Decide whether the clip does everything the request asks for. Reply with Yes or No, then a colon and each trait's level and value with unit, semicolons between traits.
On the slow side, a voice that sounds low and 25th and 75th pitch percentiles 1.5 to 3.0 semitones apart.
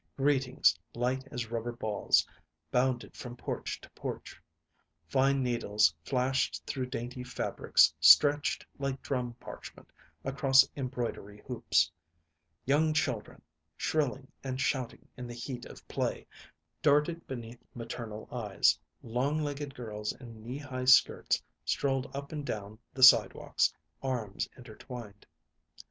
Yes: slow, 120 wpm; low, 125 Hz; narrow, 2.6 semitones